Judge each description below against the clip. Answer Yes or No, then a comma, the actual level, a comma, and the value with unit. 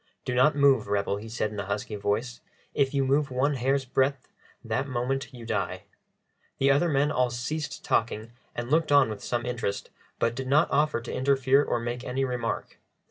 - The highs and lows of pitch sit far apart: No, average, 2.9 semitones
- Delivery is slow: No, average, 190 wpm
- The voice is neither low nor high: No, low, 125 Hz